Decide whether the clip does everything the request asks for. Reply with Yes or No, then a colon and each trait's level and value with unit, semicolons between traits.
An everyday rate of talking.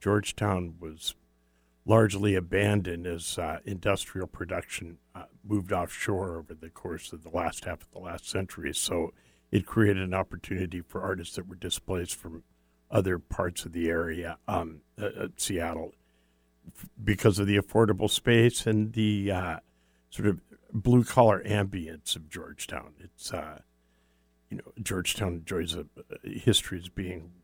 Yes: average, 145 wpm